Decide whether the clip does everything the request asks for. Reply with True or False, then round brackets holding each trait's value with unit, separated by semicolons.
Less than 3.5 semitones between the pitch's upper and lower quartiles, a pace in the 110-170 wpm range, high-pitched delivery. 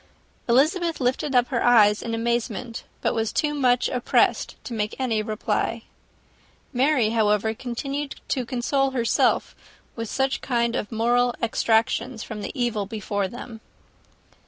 True (2.6 semitones; 135 wpm; 235 Hz)